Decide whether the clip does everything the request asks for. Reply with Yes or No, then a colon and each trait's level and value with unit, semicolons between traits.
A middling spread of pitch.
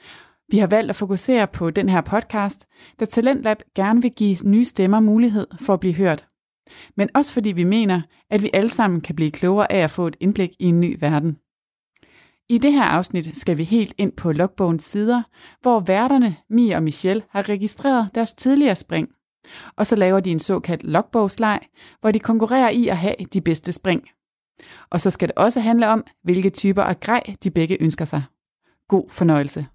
Yes: average, 4.1 semitones